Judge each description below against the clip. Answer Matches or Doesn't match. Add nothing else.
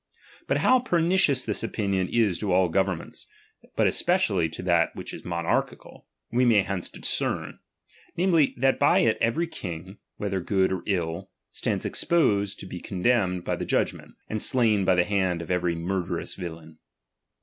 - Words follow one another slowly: Doesn't match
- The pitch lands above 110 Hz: Doesn't match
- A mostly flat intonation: Doesn't match